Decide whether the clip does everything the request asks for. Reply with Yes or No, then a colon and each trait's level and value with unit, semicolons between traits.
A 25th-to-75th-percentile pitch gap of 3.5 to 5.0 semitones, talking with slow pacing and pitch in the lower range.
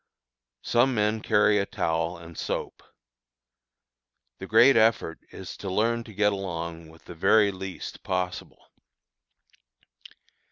Yes: average, 4.3 semitones; slow, 120 wpm; very low, 95 Hz